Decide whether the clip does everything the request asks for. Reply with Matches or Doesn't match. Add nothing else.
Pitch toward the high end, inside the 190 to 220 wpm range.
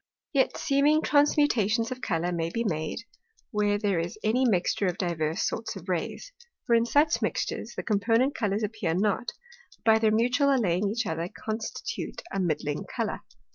Doesn't match